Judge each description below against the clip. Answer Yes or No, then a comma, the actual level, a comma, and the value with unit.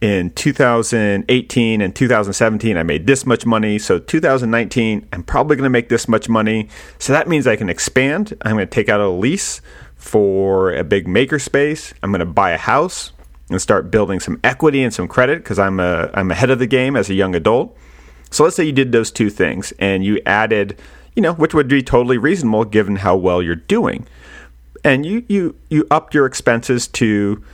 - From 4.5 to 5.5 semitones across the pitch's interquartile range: Yes, average, 5.2 semitones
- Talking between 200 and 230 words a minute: Yes, fast, 205 wpm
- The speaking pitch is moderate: No, low, 115 Hz